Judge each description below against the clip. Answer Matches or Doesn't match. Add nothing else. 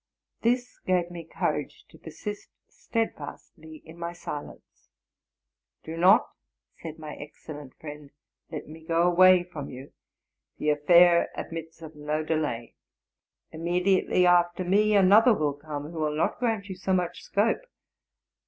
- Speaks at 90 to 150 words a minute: Matches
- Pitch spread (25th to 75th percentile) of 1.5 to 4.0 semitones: Matches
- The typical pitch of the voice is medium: Matches